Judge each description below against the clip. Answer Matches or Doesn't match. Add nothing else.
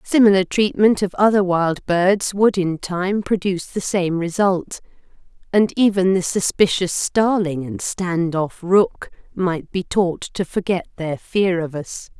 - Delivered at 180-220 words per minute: Doesn't match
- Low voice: Doesn't match